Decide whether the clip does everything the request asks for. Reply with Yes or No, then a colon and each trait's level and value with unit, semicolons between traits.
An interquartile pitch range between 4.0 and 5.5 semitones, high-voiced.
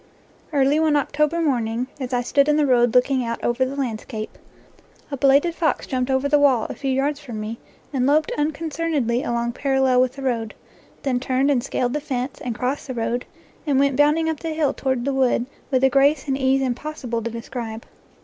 No: average, 2.8 semitones; very high, 265 Hz